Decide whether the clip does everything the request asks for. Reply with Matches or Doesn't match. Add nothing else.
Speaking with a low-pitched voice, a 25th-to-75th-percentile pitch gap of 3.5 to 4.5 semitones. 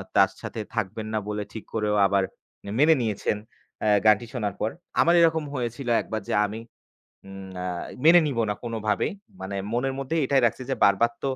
Matches